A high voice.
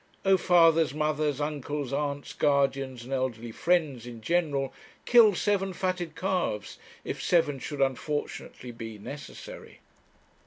No: medium, 145 Hz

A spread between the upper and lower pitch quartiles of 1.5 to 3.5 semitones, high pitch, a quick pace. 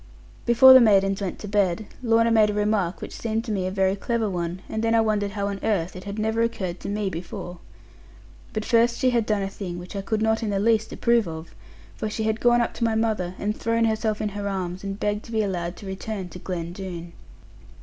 Yes: average, 2.8 semitones; high, 210 Hz; fast, 240 wpm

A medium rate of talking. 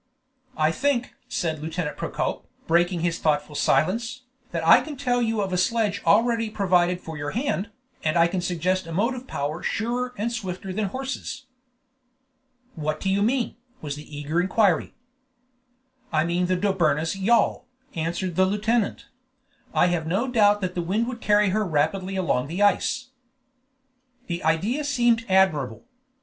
Yes: average, 160 wpm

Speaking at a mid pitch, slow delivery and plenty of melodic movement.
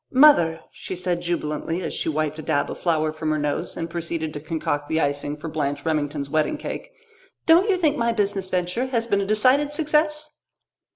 No: medium, 170 Hz; average, 195 wpm; wide, 7.3 semitones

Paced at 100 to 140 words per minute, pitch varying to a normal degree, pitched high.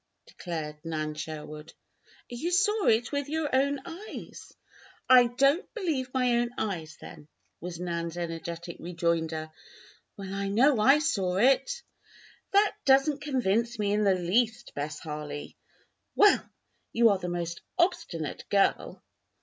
No: slow, 135 wpm; wide, 8.4 semitones; high, 205 Hz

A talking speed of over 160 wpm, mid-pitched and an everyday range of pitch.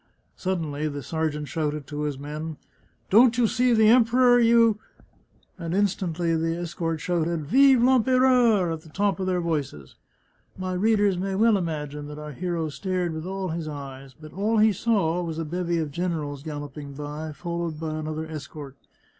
Yes: average, 185 wpm; medium, 165 Hz; average, 4.6 semitones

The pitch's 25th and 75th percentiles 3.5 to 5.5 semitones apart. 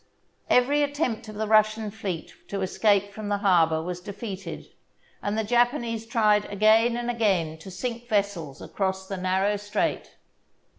No: average, 3.0 semitones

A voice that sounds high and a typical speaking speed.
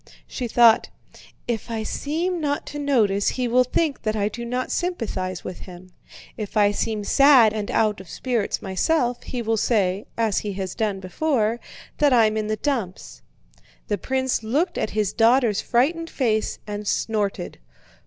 Yes: high, 225 Hz; average, 165 wpm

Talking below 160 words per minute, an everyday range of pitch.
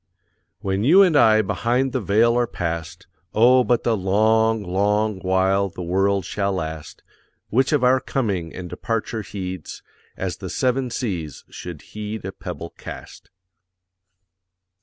Yes: average, 140 wpm; average, 4.0 semitones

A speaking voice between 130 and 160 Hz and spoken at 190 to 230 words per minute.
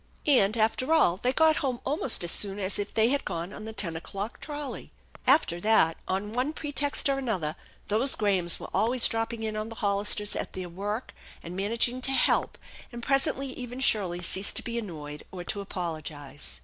No: high, 215 Hz; average, 195 wpm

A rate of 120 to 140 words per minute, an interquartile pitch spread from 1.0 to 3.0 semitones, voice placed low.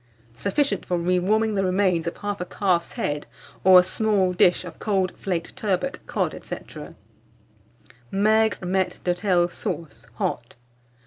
No: slow, 135 wpm; narrow, 2.5 semitones; medium, 185 Hz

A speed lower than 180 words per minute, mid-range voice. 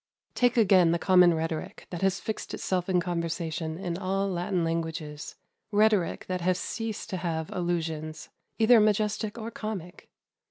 Yes: average, 150 wpm; medium, 180 Hz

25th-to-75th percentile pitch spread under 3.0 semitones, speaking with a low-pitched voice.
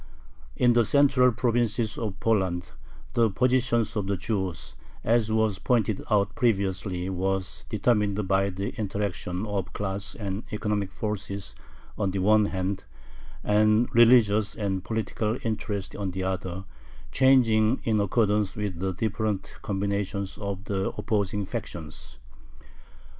Yes: narrow, 2.4 semitones; low, 105 Hz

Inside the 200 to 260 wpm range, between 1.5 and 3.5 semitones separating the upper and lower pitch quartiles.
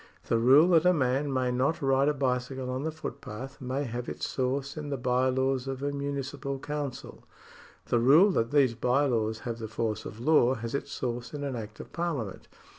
Yes: fast, 205 wpm; narrow, 2.5 semitones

